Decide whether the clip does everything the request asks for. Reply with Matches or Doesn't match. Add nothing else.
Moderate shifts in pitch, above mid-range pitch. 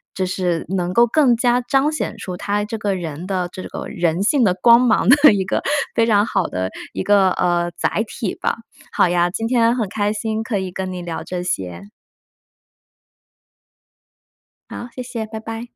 Matches